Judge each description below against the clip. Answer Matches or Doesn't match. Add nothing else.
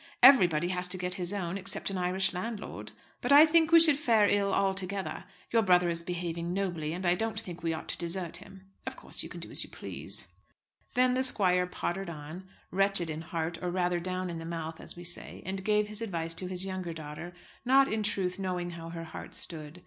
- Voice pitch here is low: Doesn't match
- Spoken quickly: Matches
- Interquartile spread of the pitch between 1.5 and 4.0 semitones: Matches